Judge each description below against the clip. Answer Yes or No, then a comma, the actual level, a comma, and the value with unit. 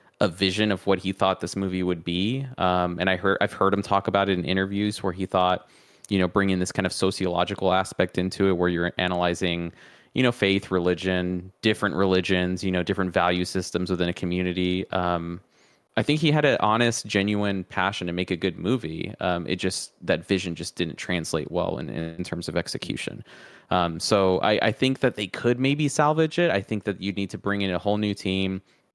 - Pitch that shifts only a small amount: Yes, narrow, 2.0 semitones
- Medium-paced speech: No, fast, 215 wpm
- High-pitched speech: No, very low, 95 Hz